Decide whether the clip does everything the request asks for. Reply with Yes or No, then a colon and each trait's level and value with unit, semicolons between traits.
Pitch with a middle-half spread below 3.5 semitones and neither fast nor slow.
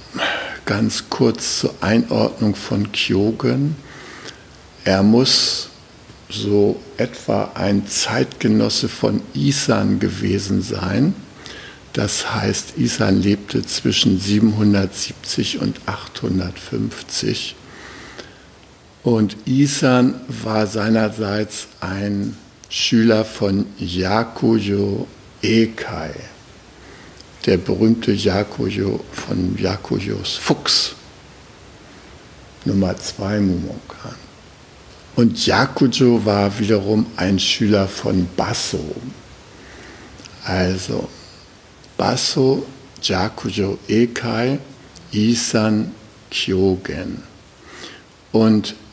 No: average, 2.9 semitones; slow, 70 wpm